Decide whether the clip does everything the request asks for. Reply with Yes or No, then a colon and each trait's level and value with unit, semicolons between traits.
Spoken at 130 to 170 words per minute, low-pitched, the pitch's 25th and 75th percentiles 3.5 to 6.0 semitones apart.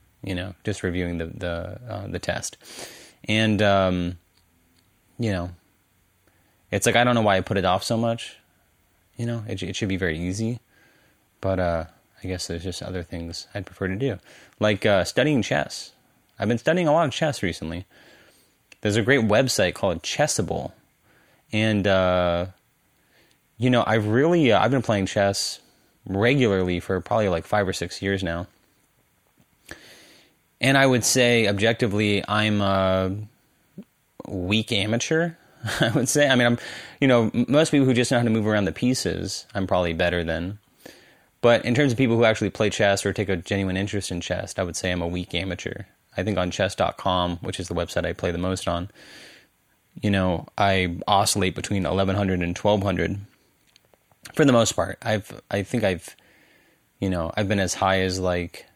No: average, 180 wpm; low, 100 Hz; average, 3.8 semitones